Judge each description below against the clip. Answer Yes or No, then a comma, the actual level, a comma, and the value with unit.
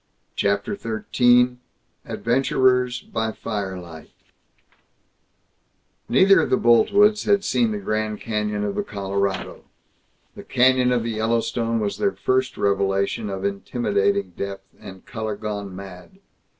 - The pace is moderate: No, slow, 120 wpm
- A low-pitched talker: Yes, low, 110 Hz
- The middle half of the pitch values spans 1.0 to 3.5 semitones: No, average, 4.0 semitones